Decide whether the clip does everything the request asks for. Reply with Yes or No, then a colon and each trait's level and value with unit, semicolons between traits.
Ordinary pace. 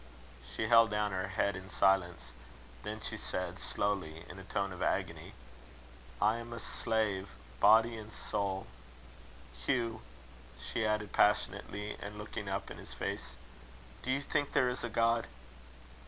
Yes: average, 150 wpm